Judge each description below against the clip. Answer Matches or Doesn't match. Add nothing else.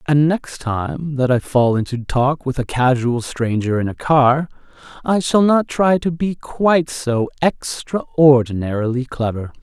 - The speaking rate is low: Doesn't match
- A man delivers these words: Matches